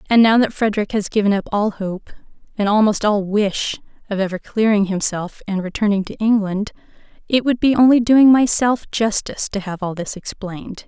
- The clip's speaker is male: No, female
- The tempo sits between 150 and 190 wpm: Yes, average, 180 wpm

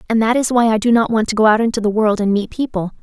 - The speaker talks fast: Yes, fast, 335 wpm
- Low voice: No, high, 220 Hz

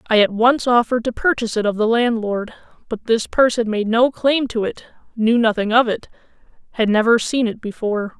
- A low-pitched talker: No, high, 230 Hz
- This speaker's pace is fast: No, average, 185 wpm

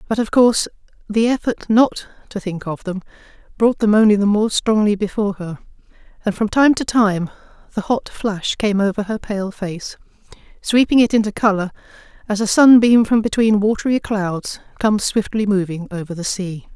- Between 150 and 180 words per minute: Yes, average, 170 wpm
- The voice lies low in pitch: No, high, 210 Hz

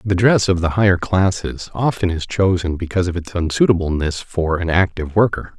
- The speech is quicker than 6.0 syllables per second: No, 5.5 syllables/s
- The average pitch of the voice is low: Yes, very low, 90 Hz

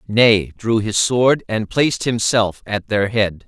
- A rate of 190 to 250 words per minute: No, average, 175 wpm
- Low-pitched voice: Yes, low, 110 Hz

